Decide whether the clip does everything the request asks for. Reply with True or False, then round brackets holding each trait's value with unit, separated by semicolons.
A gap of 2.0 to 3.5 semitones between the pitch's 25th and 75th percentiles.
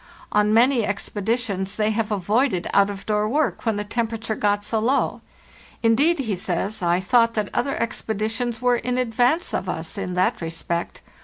True (3.1 semitones)